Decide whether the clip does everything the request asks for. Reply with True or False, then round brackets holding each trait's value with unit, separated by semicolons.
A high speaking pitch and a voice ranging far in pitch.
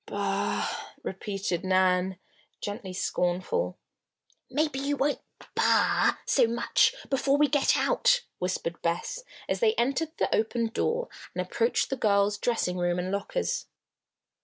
True (230 Hz; 8.0 semitones)